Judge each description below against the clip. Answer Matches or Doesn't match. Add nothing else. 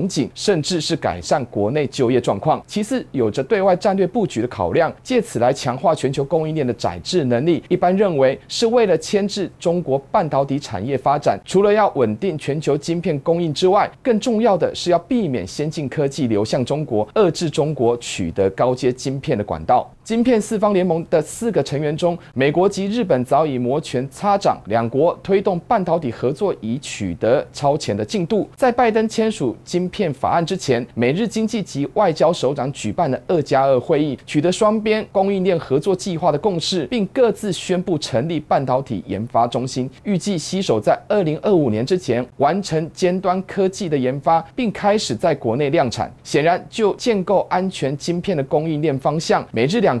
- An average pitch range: Doesn't match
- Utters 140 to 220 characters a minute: Doesn't match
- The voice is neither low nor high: Matches